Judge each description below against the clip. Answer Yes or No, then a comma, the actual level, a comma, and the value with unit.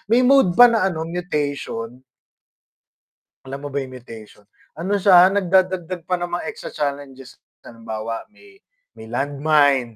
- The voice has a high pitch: No, medium, 155 Hz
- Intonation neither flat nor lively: No, wide, 5.9 semitones